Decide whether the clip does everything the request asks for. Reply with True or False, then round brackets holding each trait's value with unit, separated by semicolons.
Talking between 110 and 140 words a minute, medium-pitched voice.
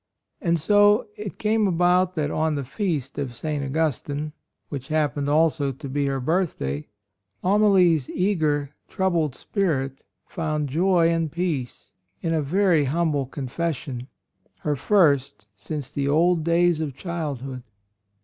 True (135 wpm; 155 Hz)